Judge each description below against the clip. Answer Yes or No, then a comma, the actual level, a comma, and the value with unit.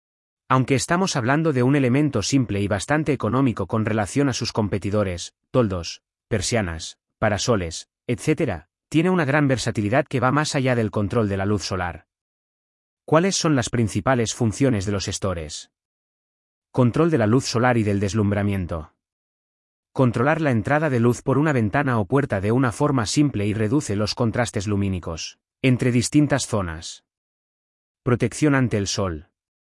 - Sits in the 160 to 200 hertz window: No, low, 115 Hz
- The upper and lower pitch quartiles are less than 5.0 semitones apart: No, wide, 5.4 semitones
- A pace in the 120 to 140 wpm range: No, average, 150 wpm